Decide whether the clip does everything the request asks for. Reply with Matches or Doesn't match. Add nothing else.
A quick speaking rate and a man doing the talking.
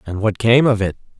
Matches